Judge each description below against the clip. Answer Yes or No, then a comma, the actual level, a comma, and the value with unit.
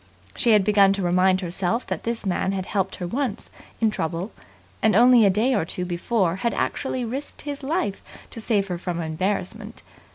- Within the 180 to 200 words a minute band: Yes, average, 190 wpm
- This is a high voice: Yes, high, 200 Hz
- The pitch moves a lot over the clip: No, average, 4.1 semitones